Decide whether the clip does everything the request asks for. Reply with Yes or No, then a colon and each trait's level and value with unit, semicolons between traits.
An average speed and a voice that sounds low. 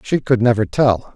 No: fast, 210 wpm; low, 120 Hz